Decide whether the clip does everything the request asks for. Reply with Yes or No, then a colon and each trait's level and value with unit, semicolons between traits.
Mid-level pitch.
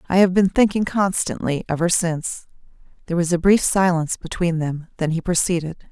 Yes: medium, 175 Hz